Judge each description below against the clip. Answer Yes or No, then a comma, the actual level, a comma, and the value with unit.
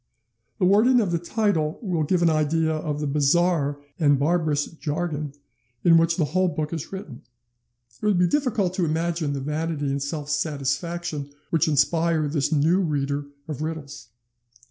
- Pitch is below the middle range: No, medium, 160 Hz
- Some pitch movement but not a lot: Yes, average, 3.0 semitones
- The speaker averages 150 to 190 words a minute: Yes, average, 165 wpm